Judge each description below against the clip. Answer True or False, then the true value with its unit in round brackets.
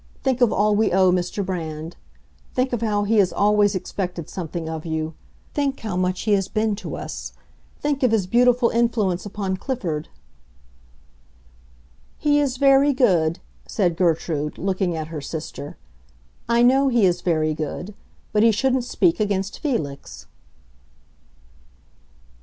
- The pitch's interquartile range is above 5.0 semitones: True (5.6 semitones)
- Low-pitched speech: False (200 Hz)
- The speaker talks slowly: False (145 wpm)